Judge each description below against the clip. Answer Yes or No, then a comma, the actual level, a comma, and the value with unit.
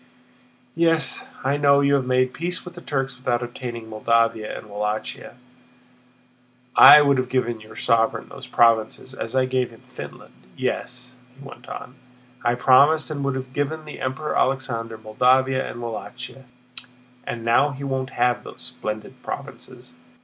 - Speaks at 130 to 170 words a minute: Yes, average, 155 wpm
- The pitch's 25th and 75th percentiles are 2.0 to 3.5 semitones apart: Yes, average, 3.0 semitones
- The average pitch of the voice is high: No, low, 130 Hz